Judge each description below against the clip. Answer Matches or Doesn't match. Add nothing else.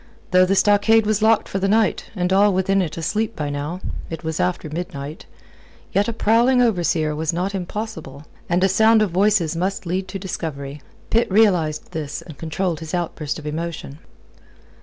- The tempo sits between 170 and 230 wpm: Matches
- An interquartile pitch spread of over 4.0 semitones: Matches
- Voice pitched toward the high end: Doesn't match